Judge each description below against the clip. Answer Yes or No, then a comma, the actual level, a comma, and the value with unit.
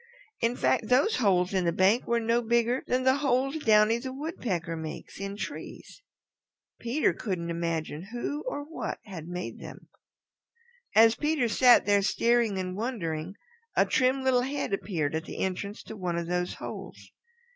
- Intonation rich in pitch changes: Yes, wide, 5.8 semitones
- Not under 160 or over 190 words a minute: Yes, average, 165 wpm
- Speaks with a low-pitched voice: No, high, 220 Hz